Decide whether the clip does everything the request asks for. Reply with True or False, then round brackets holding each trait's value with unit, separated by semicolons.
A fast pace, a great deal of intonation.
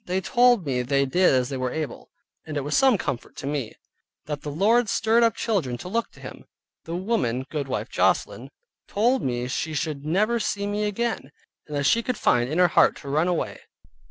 True (215 wpm; 7.6 semitones)